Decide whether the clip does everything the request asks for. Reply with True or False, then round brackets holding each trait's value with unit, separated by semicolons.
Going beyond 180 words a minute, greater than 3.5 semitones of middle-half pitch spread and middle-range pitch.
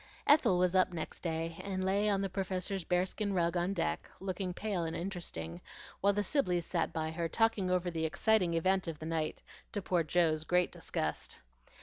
False (190 wpm; 2.8 semitones; 180 Hz)